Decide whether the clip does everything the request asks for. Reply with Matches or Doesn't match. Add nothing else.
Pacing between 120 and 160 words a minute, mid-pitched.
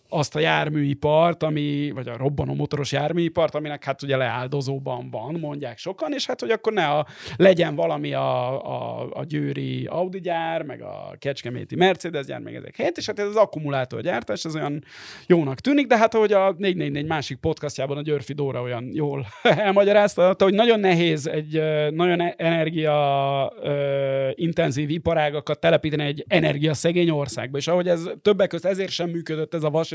Doesn't match